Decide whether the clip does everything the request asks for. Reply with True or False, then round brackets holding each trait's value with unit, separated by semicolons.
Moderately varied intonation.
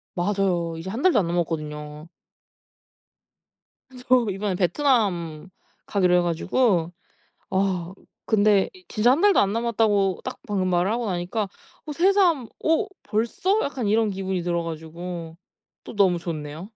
True (4.9 semitones)